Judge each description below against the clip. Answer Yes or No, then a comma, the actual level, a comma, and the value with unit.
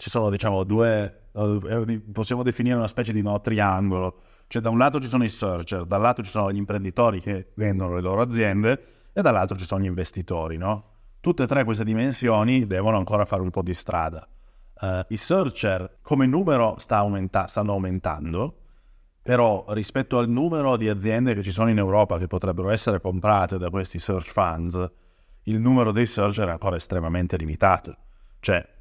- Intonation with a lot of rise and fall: No, average, 3.4 semitones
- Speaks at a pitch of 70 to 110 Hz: Yes, low, 105 Hz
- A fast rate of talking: Yes, fast, 180 wpm